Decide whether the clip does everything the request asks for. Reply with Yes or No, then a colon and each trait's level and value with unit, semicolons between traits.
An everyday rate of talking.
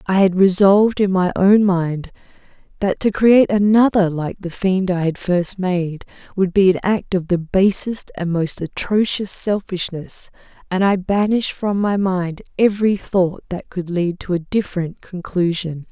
Yes: average, 165 wpm